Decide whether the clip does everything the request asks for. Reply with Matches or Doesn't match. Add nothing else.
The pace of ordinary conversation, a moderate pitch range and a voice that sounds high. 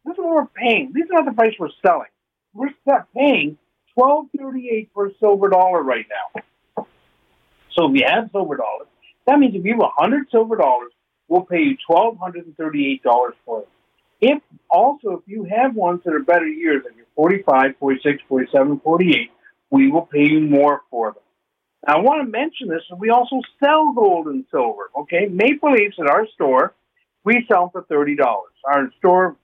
Doesn't match